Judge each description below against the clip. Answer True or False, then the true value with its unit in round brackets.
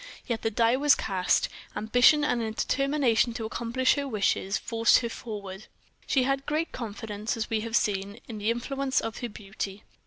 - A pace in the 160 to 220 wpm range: True (180 wpm)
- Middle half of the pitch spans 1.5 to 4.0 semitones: True (3.3 semitones)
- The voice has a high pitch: True (230 Hz)